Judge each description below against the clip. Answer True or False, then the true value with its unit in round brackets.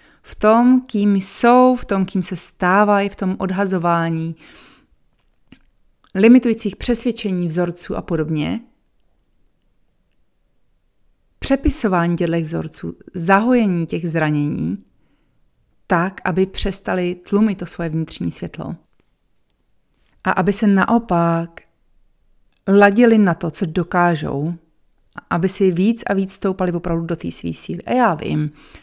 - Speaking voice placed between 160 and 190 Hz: True (185 Hz)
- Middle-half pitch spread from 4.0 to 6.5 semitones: False (3.5 semitones)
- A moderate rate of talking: False (110 wpm)